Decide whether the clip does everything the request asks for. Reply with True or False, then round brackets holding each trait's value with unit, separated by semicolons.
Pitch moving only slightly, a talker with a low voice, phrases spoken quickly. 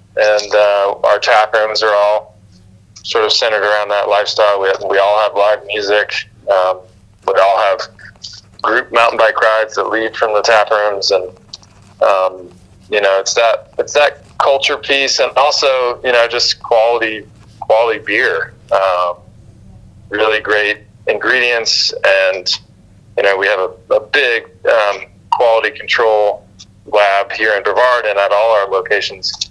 False (2.0 semitones; 105 Hz; 155 wpm)